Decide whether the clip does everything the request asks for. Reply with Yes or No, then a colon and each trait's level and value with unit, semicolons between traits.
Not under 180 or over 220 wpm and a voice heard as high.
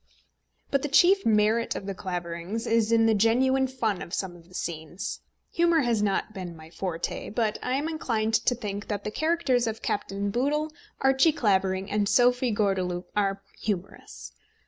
No: average, 170 wpm; high, 215 Hz